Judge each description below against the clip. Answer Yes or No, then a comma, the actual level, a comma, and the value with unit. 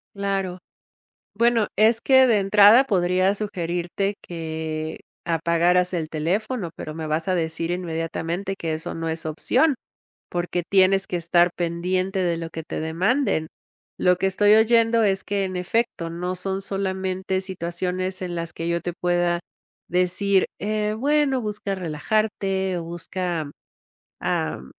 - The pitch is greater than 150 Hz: Yes, medium, 185 Hz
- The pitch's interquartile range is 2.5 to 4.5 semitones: Yes, average, 2.9 semitones